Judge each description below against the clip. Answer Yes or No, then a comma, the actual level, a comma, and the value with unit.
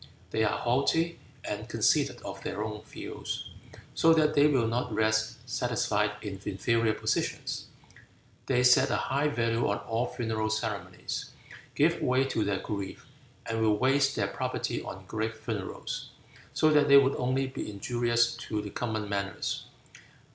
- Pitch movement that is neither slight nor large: Yes, average, 3.5 semitones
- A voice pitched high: No, low, 115 Hz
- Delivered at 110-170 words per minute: Yes, average, 155 wpm